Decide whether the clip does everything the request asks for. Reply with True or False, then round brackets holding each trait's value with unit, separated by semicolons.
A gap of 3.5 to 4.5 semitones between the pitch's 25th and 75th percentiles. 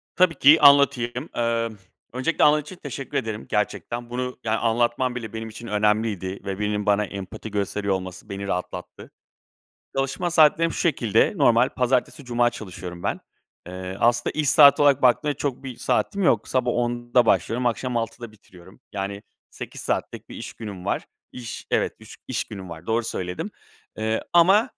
True (4.0 semitones)